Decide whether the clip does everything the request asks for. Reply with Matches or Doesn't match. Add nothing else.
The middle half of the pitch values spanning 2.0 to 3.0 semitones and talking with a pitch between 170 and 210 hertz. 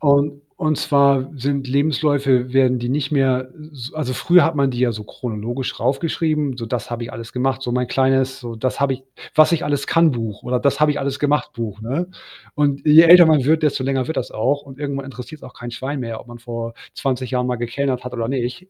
Doesn't match